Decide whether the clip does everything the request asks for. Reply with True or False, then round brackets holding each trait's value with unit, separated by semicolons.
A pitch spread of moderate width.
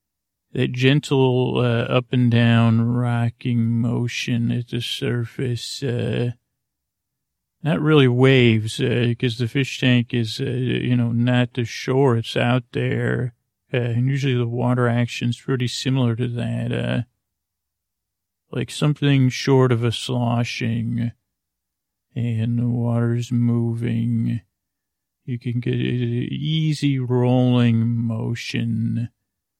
False (1.4 semitones)